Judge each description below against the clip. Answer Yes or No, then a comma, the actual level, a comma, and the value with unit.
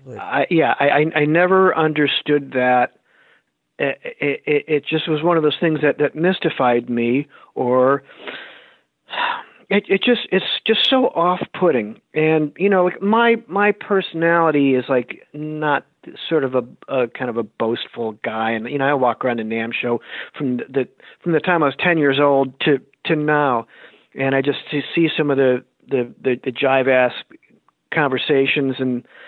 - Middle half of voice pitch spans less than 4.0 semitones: No, average, 4.7 semitones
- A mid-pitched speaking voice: Yes, medium, 145 Hz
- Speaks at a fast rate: No, average, 180 wpm